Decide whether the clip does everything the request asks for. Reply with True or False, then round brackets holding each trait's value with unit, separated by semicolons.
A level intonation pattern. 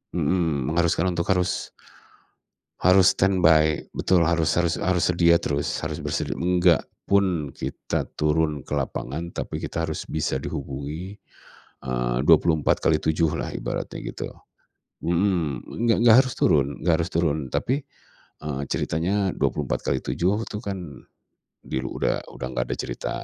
False (3.8 semitones)